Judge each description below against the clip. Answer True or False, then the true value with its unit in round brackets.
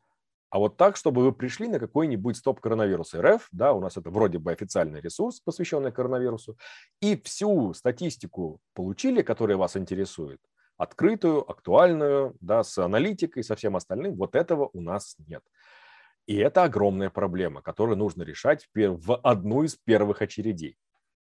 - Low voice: True (110 Hz)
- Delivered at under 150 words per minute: False (155 wpm)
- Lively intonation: True (5.8 semitones)